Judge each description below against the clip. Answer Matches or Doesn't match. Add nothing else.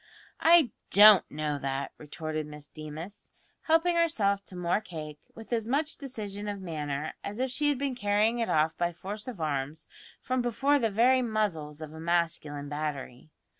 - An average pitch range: Doesn't match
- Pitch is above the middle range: Matches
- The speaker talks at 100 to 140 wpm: Doesn't match